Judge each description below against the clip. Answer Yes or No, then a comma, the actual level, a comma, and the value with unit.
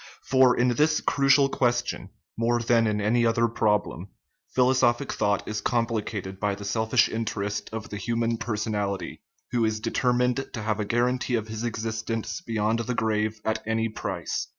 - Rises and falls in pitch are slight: Yes, narrow, 2.1 semitones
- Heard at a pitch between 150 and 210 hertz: No, low, 115 Hz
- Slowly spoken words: No, average, 165 wpm